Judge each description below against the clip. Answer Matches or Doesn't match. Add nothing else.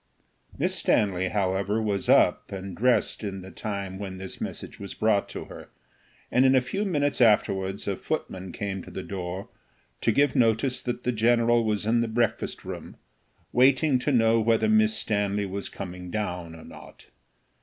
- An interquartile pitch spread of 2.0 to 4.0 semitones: Matches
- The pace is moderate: Matches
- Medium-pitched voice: Doesn't match